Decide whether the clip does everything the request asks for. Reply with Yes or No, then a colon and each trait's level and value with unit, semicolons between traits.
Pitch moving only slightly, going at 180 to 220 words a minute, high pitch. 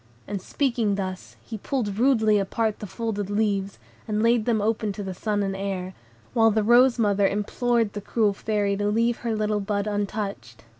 Yes: narrow, 2.1 semitones; average, 185 wpm; high, 210 Hz